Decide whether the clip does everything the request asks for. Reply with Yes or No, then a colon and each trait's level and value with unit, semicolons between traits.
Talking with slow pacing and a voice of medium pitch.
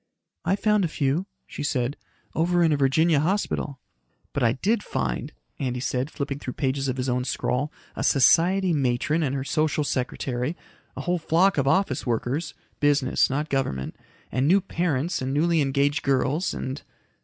No: average, 165 wpm; medium, 145 Hz